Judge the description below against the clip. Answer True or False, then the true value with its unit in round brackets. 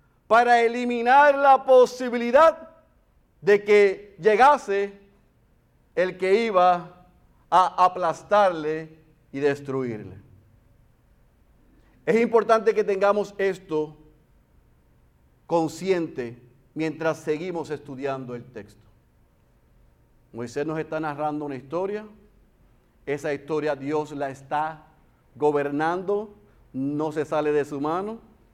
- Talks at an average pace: False (90 wpm)